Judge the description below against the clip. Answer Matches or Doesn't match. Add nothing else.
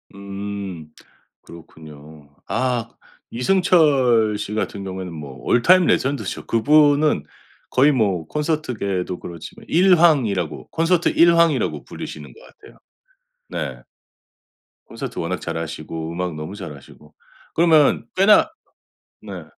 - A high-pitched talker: Doesn't match